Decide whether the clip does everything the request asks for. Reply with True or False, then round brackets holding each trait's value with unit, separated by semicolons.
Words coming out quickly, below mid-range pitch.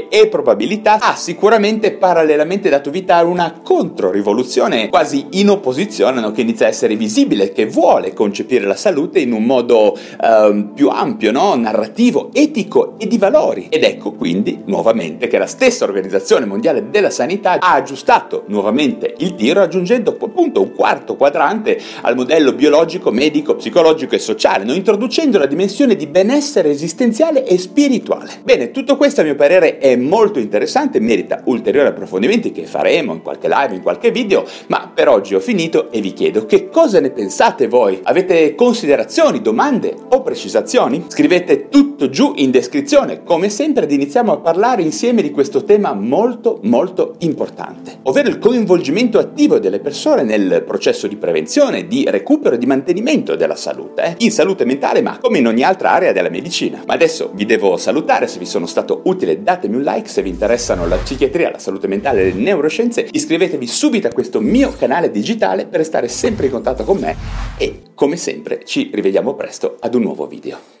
False (175 wpm; 280 Hz)